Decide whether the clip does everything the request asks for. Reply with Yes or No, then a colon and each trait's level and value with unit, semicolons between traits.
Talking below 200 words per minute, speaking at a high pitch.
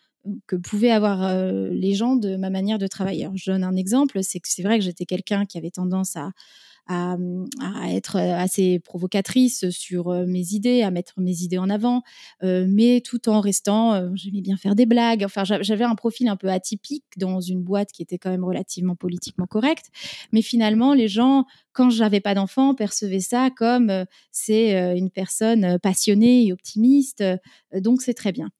Yes: average, 180 wpm; high, 200 Hz